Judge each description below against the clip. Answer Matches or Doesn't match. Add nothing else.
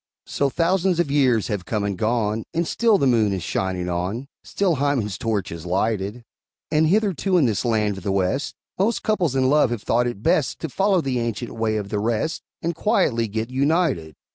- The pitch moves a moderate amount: Doesn't match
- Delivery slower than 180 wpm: Doesn't match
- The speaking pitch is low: Matches